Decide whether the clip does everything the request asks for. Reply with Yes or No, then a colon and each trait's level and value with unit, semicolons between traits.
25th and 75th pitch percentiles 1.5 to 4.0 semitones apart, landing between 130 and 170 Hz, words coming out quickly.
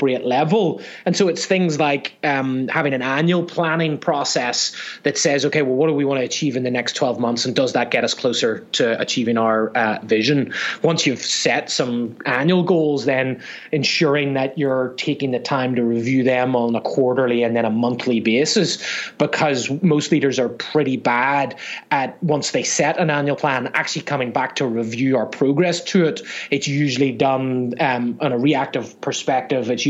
No: average, 3.4 semitones; low, 135 Hz; average, 185 wpm